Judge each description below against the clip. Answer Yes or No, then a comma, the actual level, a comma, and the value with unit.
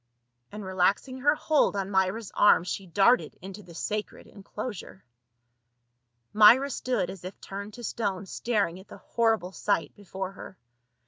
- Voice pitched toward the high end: Yes, high, 200 Hz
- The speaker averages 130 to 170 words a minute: Yes, average, 150 wpm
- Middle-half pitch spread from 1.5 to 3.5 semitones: Yes, average, 3.1 semitones